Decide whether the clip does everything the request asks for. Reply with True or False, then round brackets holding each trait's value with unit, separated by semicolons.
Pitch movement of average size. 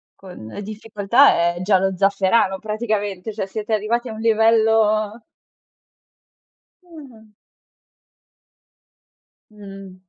False (2.3 semitones)